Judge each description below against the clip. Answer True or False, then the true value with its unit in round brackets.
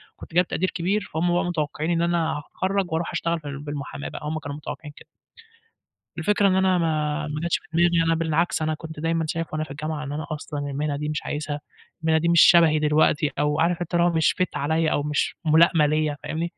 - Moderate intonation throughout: False (2.1 semitones)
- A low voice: False (160 Hz)